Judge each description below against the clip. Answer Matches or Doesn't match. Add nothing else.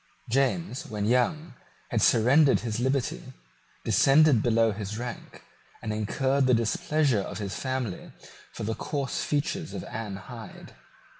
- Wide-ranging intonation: Doesn't match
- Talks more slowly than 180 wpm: Matches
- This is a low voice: Matches